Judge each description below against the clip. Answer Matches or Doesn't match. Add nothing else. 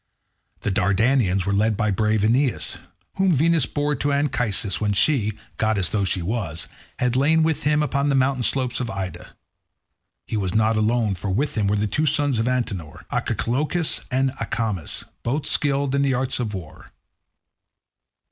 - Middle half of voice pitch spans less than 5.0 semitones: Doesn't match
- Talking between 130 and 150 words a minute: Doesn't match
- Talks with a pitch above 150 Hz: Doesn't match